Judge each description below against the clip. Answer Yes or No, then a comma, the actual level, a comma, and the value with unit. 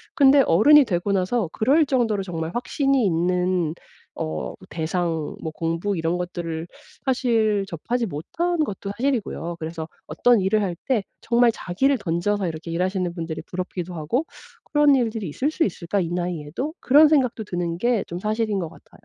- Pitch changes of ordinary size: No, wide, 6.2 semitones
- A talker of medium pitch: No, high, 195 Hz